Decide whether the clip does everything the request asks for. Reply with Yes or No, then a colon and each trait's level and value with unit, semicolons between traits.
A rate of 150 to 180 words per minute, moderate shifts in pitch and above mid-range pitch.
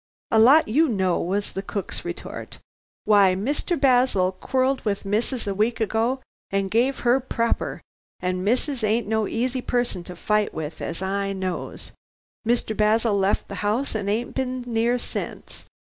Yes: average, 160 wpm; average, 3.8 semitones; high, 220 Hz